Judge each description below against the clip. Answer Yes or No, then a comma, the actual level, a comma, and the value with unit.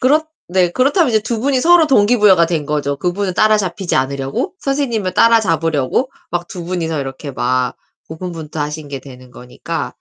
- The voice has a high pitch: No, medium, 175 Hz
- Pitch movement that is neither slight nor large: No, wide, 7.9 semitones